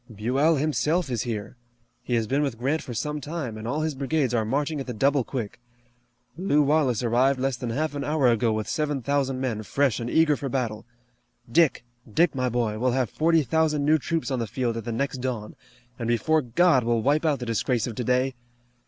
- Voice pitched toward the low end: Yes, low, 130 Hz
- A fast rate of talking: Yes, fast, 215 wpm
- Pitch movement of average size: Yes, average, 4.0 semitones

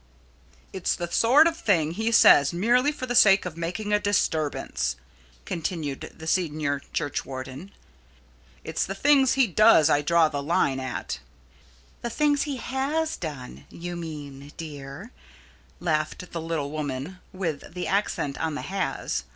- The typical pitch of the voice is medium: Yes, medium, 170 Hz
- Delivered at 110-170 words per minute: Yes, average, 145 wpm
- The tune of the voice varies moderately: No, wide, 6.4 semitones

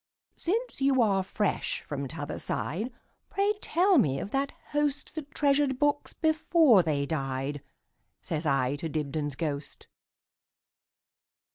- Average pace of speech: No, slow, 110 wpm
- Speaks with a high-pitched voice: Yes, high, 200 Hz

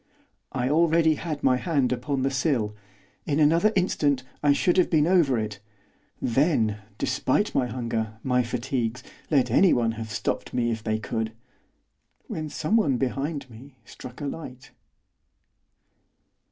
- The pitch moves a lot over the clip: No, average, 4.5 semitones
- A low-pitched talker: Yes, low, 130 Hz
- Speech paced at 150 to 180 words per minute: No, average, 140 wpm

